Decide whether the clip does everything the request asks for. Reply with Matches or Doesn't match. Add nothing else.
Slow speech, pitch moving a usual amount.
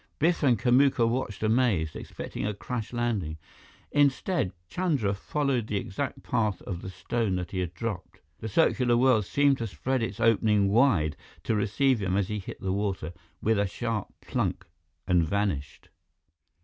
Doesn't match